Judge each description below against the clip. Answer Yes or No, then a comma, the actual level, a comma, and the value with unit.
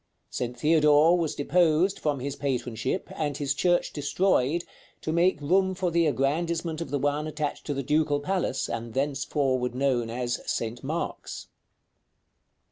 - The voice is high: No, medium, 145 Hz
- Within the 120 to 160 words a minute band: Yes, average, 145 wpm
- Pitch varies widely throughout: No, average, 3.7 semitones